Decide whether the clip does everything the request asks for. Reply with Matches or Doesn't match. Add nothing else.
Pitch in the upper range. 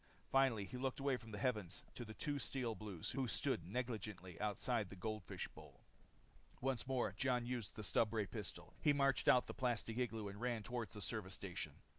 Doesn't match